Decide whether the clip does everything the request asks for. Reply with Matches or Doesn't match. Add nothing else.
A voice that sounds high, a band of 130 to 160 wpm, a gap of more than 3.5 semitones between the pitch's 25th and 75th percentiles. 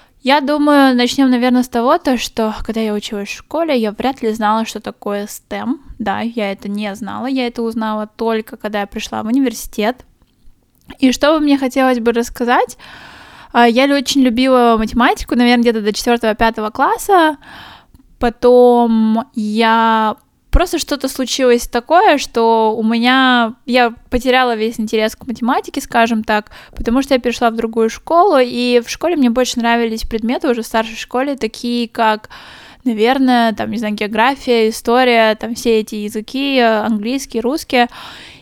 Doesn't match